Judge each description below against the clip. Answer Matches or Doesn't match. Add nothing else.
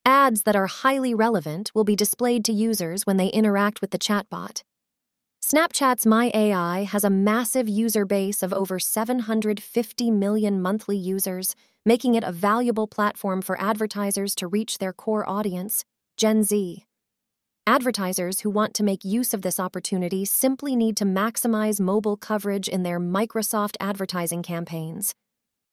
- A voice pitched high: Matches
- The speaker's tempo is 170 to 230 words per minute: Doesn't match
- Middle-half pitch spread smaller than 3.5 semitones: Matches